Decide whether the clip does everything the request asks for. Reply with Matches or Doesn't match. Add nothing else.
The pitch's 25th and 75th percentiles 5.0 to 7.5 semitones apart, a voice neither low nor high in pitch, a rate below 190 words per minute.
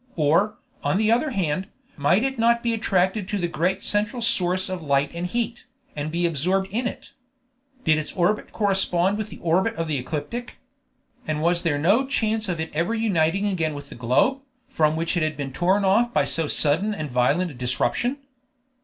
Doesn't match